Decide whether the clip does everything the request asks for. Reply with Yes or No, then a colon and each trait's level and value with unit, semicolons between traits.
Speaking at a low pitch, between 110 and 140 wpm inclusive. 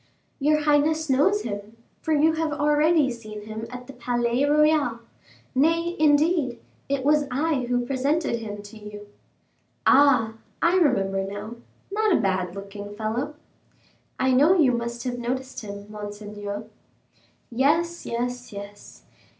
No: very high, 250 Hz; slow, 135 wpm